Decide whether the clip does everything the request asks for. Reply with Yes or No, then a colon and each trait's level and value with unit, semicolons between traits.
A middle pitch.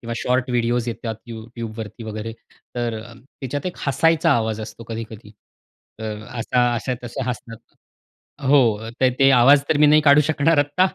No: low, 120 Hz